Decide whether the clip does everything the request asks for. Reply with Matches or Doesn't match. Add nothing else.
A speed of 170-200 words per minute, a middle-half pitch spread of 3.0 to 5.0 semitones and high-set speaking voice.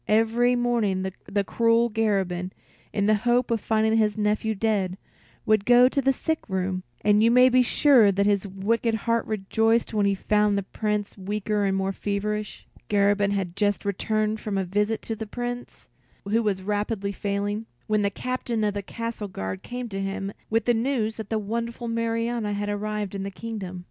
Doesn't match